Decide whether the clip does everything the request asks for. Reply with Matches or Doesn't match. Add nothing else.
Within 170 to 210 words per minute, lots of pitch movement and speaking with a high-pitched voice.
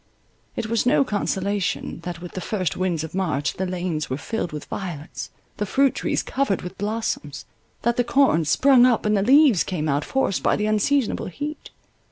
Matches